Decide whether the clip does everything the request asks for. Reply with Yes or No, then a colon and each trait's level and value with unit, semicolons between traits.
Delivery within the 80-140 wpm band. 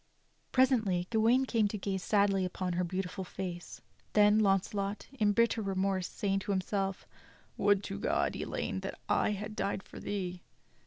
No: average, 155 wpm